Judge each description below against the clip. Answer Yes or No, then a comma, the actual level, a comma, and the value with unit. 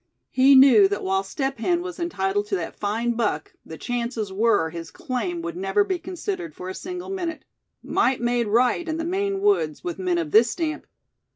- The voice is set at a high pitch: Yes, high, 245 Hz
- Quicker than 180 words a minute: Yes, average, 195 wpm